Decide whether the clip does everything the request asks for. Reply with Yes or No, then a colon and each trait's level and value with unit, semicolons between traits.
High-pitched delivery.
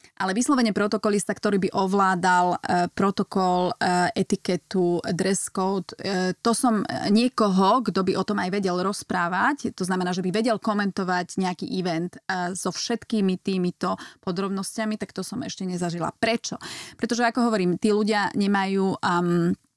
Yes: high, 195 Hz